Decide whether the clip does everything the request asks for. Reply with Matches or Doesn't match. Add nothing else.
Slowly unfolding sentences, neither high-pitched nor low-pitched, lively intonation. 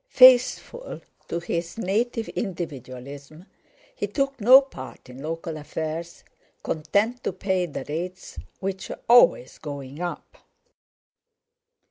Matches